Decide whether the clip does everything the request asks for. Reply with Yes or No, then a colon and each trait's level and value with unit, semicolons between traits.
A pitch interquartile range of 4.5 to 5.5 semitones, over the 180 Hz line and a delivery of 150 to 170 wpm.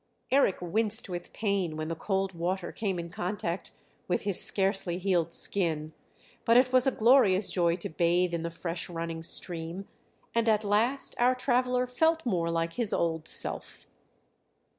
Yes: average, 5.0 semitones; high, 190 Hz; average, 160 wpm